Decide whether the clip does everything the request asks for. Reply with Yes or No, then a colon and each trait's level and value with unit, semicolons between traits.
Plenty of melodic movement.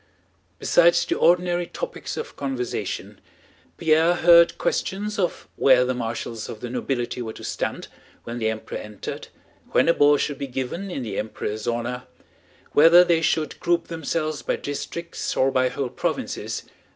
Yes: wide, 5.7 semitones